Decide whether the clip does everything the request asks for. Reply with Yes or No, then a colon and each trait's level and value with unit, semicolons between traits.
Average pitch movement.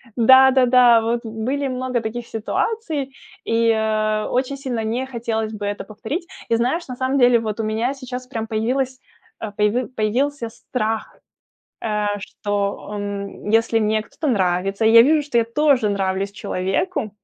Yes: average, 3.2 semitones